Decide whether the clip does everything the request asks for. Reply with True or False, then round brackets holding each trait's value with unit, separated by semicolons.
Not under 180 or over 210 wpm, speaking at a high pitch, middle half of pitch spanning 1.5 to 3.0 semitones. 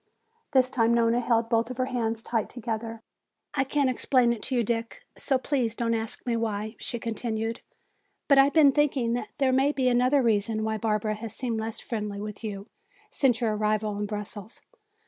True (185 wpm; 230 Hz; 2.6 semitones)